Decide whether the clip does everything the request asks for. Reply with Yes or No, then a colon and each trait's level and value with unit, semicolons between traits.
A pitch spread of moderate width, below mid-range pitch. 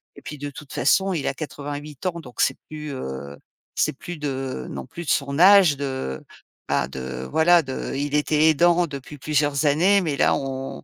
No: average, 3.0 semitones; medium, 145 Hz